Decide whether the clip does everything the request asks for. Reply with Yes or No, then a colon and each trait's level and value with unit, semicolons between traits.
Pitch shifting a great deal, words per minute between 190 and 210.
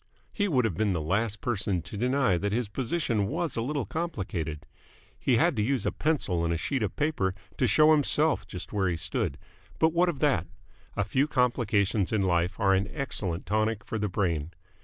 Yes: wide, 6.5 semitones; average, 200 wpm